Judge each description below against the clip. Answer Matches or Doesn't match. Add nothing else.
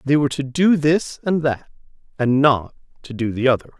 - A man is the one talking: Matches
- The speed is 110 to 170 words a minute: Doesn't match